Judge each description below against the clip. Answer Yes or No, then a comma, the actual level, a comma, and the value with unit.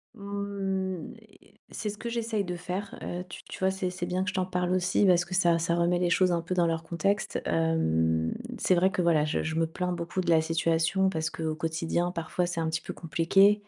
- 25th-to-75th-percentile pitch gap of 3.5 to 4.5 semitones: No, narrow, 2.5 semitones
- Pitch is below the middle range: No, medium, 175 Hz